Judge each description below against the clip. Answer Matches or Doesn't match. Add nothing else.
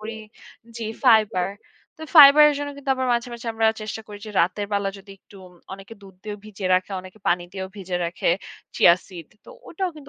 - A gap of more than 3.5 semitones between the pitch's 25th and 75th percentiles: Matches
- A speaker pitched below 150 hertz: Doesn't match